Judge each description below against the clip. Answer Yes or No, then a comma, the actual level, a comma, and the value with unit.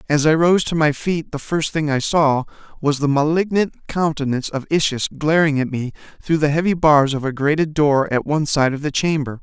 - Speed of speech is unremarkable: No, fast, 215 wpm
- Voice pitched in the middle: Yes, medium, 150 Hz